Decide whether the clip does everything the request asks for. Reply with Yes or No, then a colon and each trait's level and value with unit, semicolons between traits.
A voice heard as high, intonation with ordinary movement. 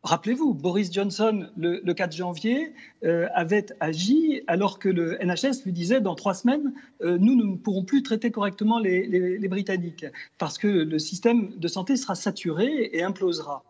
Yes: high, 195 Hz; average, 4.6 semitones